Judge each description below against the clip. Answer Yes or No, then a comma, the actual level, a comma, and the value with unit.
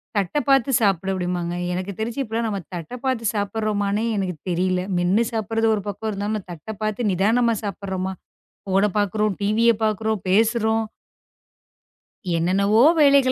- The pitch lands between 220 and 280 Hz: No, high, 210 Hz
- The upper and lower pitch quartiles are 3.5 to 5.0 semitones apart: No, average, 2.8 semitones